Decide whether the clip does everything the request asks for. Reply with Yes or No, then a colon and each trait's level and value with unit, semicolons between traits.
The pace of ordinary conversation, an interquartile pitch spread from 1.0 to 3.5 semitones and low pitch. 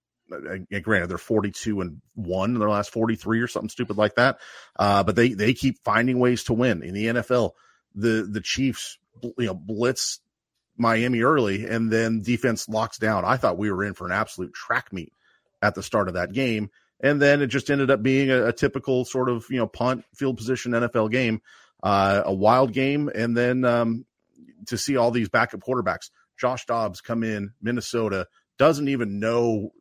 Yes: average, 195 wpm; average, 3.2 semitones; low, 115 Hz